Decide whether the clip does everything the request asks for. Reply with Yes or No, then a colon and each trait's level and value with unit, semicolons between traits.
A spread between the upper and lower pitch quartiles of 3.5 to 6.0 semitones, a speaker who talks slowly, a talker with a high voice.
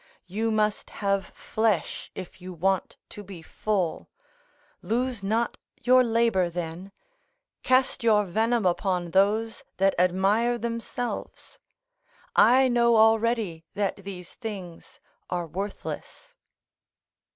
Yes: average, 3.9 semitones; slow, 105 wpm; high, 205 Hz